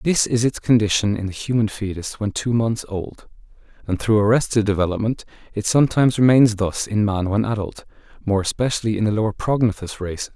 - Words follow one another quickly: No, average, 180 wpm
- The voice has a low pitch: Yes, low, 110 Hz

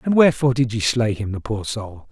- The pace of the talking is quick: Yes, fast, 255 wpm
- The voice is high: No, low, 115 Hz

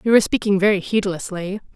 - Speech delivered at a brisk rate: No, average, 170 wpm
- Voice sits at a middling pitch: No, high, 195 Hz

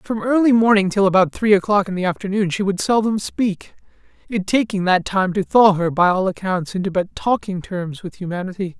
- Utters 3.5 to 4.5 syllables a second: No, 5.4 syllables/s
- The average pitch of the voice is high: Yes, high, 195 Hz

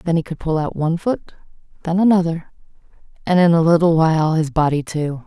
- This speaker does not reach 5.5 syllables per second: No, 6.0 syllables/s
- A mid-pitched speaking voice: Yes, medium, 165 Hz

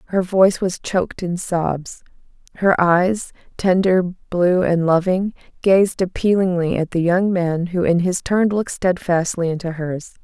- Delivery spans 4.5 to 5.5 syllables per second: No, 4.2 syllables/s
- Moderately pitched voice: Yes, medium, 180 Hz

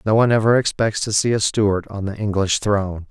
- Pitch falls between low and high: No, low, 105 Hz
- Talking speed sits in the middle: No, fast, 230 wpm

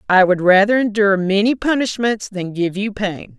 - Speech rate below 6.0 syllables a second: Yes, 5.0 syllables/s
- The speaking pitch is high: Yes, high, 200 Hz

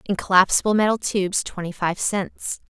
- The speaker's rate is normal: Yes, average, 155 wpm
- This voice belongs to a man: No, female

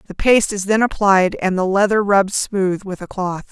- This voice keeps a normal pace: No, fast, 220 wpm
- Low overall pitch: No, high, 195 Hz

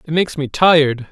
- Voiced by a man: Yes, male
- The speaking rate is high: Yes, fast, 215 wpm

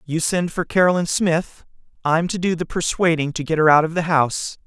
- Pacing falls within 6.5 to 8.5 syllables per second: No, 5.6 syllables/s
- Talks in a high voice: No, medium, 165 Hz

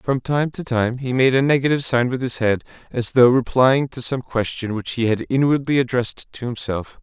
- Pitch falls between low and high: No, low, 125 Hz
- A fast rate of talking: Yes, fast, 215 wpm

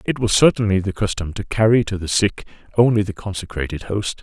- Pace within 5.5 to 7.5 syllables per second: Yes, 5.8 syllables/s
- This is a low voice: Yes, low, 100 Hz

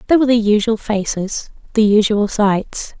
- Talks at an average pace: Yes, average, 160 wpm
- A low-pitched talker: No, high, 215 Hz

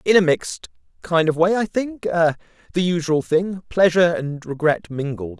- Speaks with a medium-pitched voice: Yes, medium, 165 Hz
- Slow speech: No, average, 165 wpm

